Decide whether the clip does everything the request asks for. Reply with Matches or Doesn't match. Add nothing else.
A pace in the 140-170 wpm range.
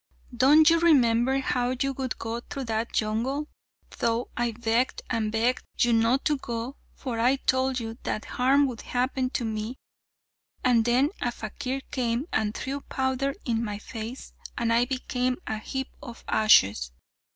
Matches